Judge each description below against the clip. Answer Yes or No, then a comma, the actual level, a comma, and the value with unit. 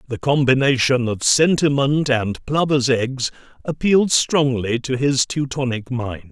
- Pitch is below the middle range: Yes, low, 130 Hz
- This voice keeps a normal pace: No, slow, 125 wpm